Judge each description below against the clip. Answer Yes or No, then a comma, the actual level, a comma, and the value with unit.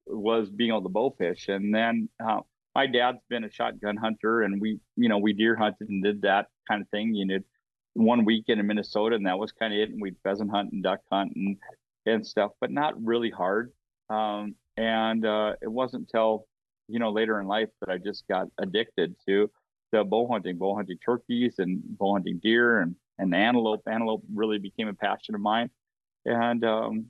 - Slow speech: No, fast, 205 wpm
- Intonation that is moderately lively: No, narrow, 1.8 semitones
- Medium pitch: No, low, 110 Hz